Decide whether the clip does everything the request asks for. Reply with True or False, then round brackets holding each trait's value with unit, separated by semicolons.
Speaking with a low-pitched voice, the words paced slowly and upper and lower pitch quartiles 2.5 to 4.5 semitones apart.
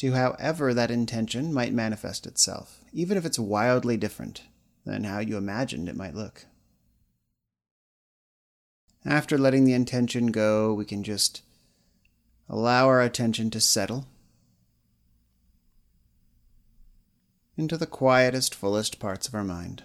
True (115 Hz; 120 wpm; 3.9 semitones)